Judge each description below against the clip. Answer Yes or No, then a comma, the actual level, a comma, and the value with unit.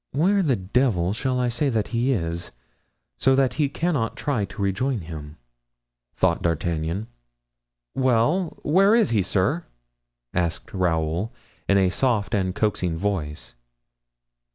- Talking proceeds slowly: Yes, slow, 130 wpm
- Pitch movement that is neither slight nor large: No, wide, 6.9 semitones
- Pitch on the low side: Yes, low, 105 Hz